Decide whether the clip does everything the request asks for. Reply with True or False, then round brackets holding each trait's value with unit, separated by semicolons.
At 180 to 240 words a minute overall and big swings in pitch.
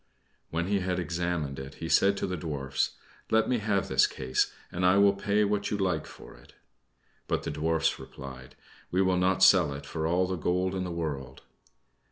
False (200 wpm; 3.8 semitones)